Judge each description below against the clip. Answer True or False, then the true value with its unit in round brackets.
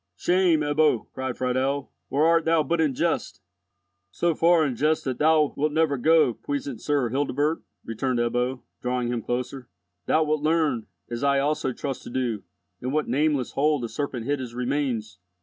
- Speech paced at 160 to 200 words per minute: True (165 wpm)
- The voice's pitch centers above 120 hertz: True (140 Hz)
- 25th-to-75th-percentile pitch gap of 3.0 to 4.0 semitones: True (3.7 semitones)